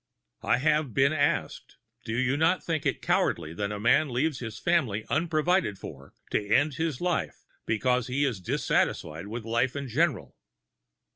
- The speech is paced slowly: No, average, 160 wpm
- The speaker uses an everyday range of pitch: No, wide, 5.9 semitones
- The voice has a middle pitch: No, low, 130 Hz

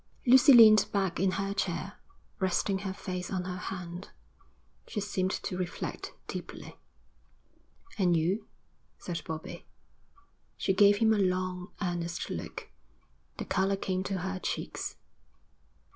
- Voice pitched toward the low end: No, high, 190 Hz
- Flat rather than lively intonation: Yes, narrow, 1.7 semitones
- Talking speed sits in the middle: No, slow, 130 wpm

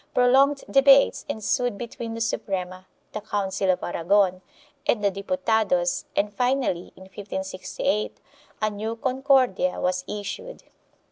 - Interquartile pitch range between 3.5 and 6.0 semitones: Yes, average, 4.7 semitones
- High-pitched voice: Yes, high, 210 Hz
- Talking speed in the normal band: No, slow, 120 wpm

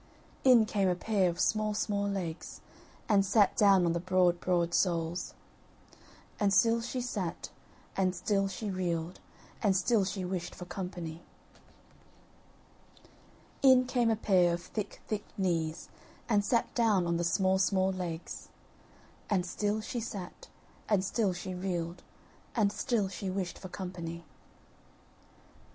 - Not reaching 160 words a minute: Yes, average, 140 wpm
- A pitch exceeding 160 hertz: Yes, high, 190 Hz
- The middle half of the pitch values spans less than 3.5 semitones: Yes, average, 2.9 semitones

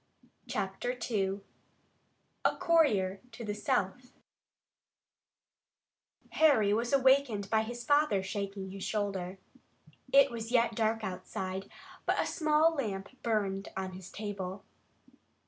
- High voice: Yes, high, 210 Hz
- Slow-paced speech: Yes, slow, 110 wpm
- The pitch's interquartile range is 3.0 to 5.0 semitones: Yes, average, 4.1 semitones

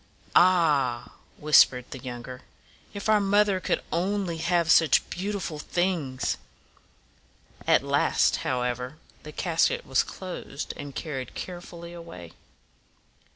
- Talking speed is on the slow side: Yes, slow, 125 wpm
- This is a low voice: No, medium, 160 Hz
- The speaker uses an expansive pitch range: Yes, wide, 5.9 semitones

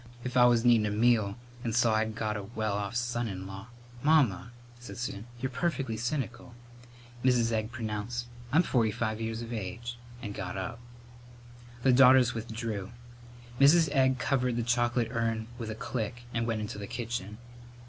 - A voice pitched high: No, low, 115 Hz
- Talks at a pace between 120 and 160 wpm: No, average, 175 wpm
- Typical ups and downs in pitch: No, narrow, 2.1 semitones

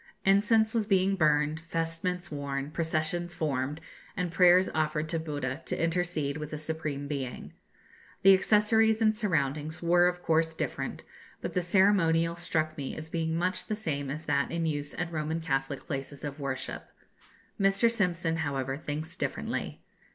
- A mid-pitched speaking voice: Yes, medium, 160 Hz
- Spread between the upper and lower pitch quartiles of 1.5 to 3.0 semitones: No, average, 3.4 semitones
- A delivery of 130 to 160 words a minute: Yes, average, 155 wpm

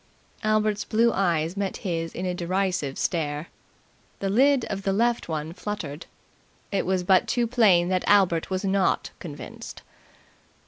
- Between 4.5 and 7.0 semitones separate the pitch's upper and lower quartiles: No, average, 3.4 semitones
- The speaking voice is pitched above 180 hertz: Yes, high, 190 Hz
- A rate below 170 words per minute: Yes, average, 145 wpm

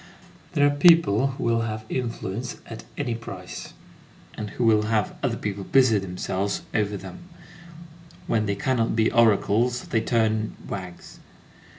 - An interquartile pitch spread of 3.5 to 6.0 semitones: No, average, 3.0 semitones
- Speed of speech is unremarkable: Yes, average, 145 wpm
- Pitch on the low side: Yes, low, 110 Hz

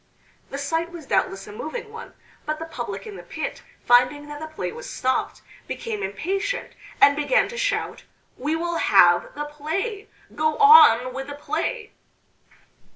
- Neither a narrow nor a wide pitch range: No, wide, 6.8 semitones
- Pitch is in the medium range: No, very high, 310 Hz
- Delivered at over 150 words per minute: Yes, average, 160 wpm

